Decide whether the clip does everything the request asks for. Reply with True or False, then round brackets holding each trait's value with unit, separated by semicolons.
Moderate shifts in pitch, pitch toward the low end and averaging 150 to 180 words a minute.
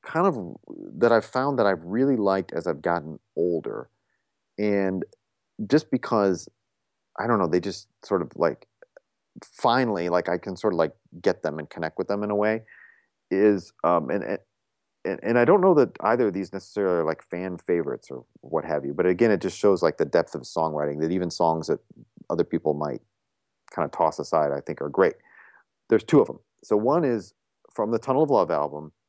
False (4.3 semitones; 95 Hz; 205 wpm)